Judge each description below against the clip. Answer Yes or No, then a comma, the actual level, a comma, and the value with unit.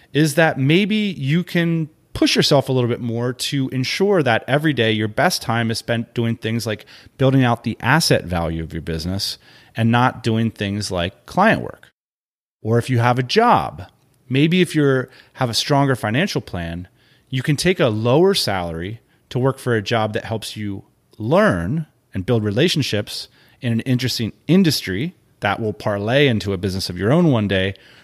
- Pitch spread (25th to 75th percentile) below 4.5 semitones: No, average, 5.1 semitones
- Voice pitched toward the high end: No, low, 120 Hz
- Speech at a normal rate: Yes, average, 185 wpm